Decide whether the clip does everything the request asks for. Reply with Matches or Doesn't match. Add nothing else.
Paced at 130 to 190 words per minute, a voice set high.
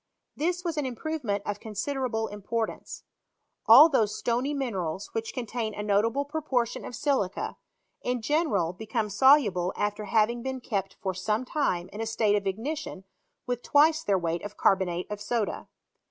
Matches